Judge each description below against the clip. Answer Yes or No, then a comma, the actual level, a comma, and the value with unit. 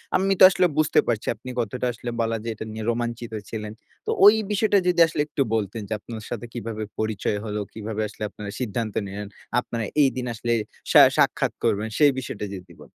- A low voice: Yes, low, 115 Hz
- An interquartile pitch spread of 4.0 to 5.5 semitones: No, average, 2.9 semitones